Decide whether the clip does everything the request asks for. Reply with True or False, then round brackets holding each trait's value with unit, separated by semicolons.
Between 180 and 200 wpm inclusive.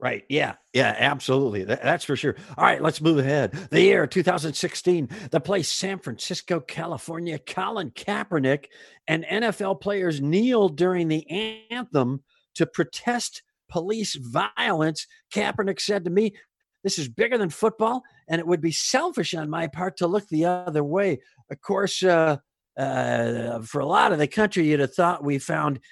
False (165 wpm)